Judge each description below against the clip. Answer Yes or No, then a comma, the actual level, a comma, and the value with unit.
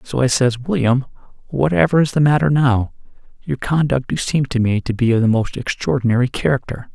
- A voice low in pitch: Yes, low, 130 Hz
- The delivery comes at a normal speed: Yes, average, 190 wpm